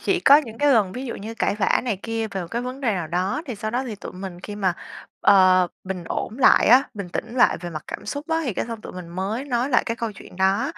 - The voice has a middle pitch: No, high, 215 Hz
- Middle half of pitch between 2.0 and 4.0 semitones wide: No, average, 4.7 semitones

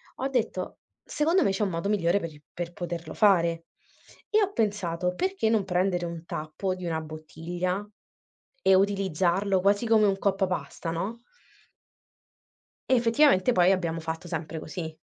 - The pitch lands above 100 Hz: Yes, medium, 185 Hz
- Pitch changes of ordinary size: Yes, average, 3.5 semitones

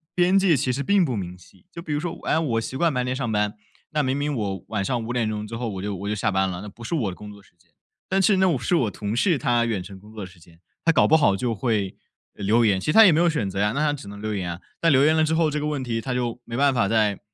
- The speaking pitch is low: Yes, low, 120 Hz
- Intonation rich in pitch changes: Yes, wide, 6.5 semitones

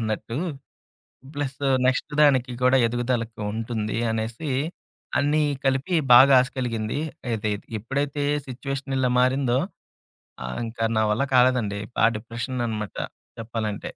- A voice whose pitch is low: Yes, low, 125 Hz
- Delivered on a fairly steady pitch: No, average, 3.0 semitones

